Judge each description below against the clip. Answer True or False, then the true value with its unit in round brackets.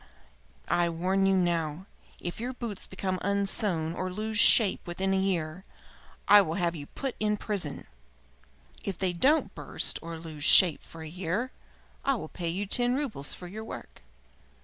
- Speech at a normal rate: True (170 wpm)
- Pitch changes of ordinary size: True (3.8 semitones)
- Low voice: False (185 Hz)